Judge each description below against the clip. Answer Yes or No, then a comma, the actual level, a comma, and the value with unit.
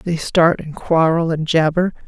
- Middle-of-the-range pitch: Yes, medium, 165 Hz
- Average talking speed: Yes, average, 175 wpm